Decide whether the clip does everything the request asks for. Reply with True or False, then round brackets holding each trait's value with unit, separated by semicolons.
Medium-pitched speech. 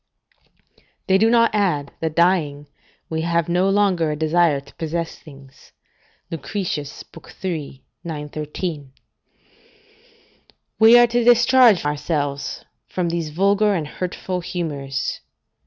True (170 Hz)